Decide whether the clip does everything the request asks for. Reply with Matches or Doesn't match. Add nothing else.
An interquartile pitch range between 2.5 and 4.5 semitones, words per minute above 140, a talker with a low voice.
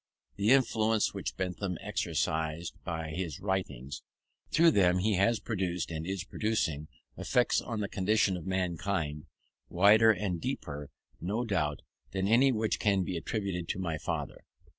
Matches